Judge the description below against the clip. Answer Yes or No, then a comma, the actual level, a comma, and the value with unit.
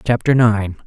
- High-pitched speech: No, low, 110 Hz